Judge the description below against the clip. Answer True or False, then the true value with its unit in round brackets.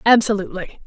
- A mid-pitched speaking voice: False (205 Hz)